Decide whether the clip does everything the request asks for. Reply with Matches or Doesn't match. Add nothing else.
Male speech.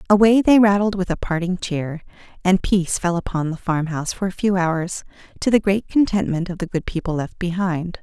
Doesn't match